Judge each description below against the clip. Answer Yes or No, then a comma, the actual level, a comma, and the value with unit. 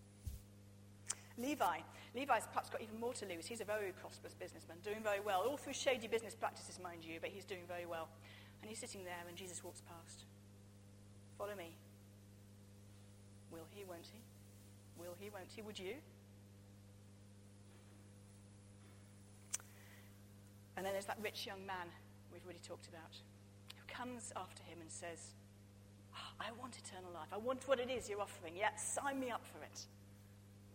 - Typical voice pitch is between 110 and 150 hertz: No, low, 100 Hz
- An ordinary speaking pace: Yes, average, 165 wpm